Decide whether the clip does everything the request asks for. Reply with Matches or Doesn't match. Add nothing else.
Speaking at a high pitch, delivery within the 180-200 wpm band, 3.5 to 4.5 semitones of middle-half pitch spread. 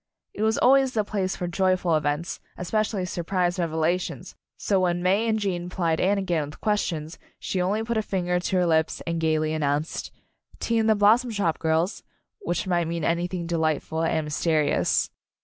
Doesn't match